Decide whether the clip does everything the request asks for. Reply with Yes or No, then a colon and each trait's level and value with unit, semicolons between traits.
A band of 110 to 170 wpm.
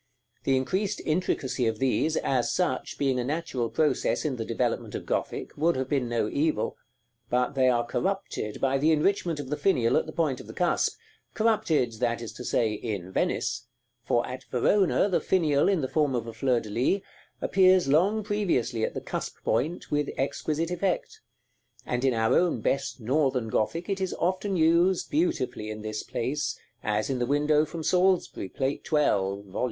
No: average, 185 wpm